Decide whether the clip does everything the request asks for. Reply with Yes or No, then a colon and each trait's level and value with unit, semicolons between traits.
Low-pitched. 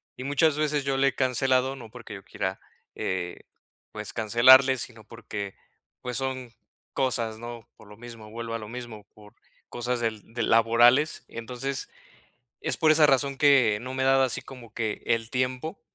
Yes: low, 120 Hz